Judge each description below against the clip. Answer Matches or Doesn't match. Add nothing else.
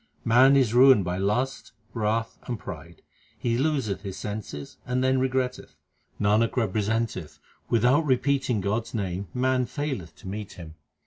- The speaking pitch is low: Matches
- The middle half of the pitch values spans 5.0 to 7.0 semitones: Doesn't match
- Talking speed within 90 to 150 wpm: Matches